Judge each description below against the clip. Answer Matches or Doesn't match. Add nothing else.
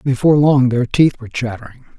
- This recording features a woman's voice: Doesn't match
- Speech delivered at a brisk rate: Doesn't match